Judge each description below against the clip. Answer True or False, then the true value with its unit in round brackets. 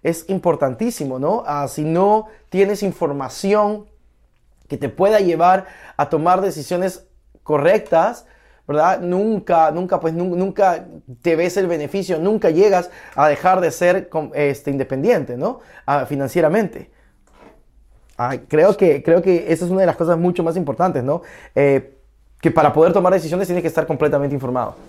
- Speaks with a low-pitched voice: False (175 Hz)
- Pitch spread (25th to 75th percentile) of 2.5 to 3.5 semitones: False (4.0 semitones)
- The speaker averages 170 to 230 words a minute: False (150 wpm)